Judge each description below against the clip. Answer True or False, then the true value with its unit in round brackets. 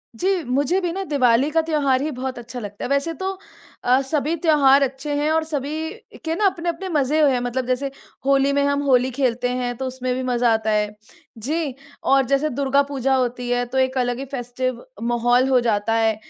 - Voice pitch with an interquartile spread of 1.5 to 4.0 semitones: True (3.1 semitones)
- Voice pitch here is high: True (265 Hz)